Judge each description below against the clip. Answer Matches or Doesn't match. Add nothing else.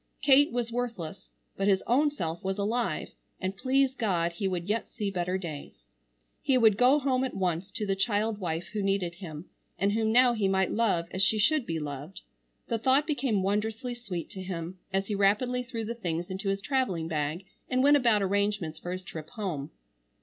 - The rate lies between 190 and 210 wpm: Matches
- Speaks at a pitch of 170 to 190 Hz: Doesn't match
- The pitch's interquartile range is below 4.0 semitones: Doesn't match